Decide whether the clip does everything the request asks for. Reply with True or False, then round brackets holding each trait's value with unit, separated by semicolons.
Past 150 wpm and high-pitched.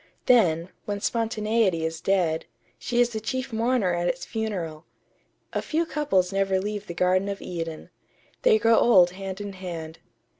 True (160 wpm; 195 Hz)